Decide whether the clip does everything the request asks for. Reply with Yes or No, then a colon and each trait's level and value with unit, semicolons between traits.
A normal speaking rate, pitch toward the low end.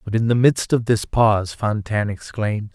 Yes: average, 195 wpm; low, 105 Hz